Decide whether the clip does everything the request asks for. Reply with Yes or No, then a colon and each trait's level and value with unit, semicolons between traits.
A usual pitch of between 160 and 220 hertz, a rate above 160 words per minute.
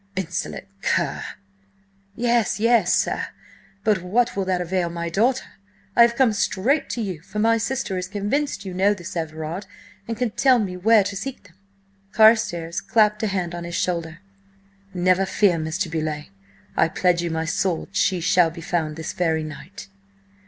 Yes: medium, 185 Hz; average, 175 wpm